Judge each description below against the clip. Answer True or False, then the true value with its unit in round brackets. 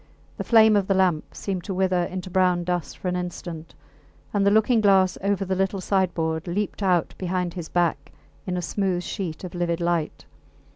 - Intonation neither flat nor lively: False (1.9 semitones)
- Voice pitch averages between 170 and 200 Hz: True (185 Hz)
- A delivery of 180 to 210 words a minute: True (190 wpm)